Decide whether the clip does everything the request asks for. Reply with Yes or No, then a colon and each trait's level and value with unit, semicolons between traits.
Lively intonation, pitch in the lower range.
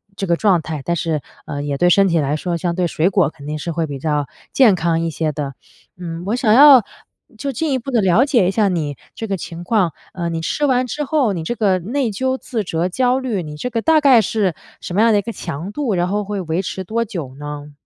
No: wide, 5.9 semitones; medium, 185 Hz